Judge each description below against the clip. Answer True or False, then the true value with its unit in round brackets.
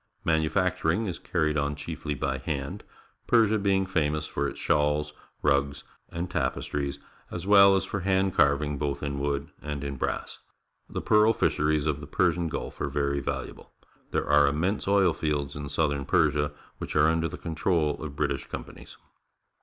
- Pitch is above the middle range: False (75 Hz)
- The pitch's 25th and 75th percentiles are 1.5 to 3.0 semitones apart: False (3.8 semitones)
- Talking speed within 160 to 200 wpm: True (170 wpm)